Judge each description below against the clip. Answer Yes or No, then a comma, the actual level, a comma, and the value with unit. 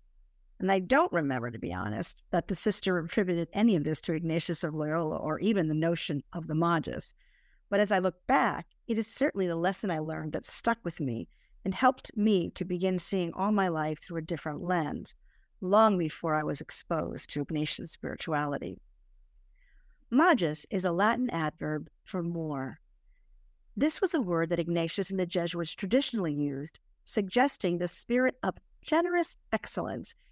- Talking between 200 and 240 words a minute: No, average, 170 wpm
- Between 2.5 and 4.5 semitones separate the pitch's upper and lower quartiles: No, average, 4.9 semitones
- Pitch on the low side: No, medium, 180 Hz